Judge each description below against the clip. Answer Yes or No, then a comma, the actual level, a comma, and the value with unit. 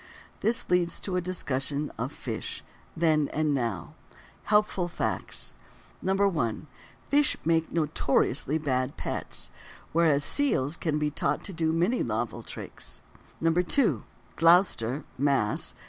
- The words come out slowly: Yes, slow, 115 wpm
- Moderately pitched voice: Yes, medium, 160 Hz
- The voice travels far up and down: No, average, 4.1 semitones